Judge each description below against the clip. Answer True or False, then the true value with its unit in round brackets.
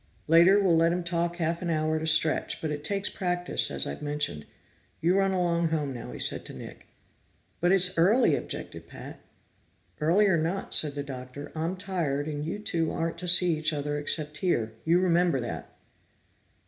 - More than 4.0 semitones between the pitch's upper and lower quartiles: False (3.1 semitones)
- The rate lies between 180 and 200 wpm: True (190 wpm)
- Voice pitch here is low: False (165 Hz)